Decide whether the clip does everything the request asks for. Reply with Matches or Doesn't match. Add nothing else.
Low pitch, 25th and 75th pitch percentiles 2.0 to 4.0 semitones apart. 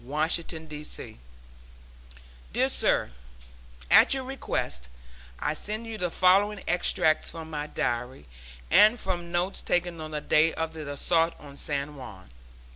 Doesn't match